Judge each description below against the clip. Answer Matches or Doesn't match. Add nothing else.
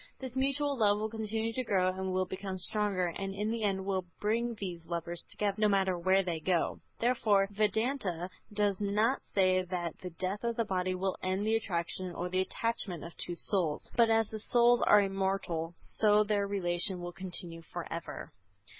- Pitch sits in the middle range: Doesn't match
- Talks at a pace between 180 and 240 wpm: Matches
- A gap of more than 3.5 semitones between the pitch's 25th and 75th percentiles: Doesn't match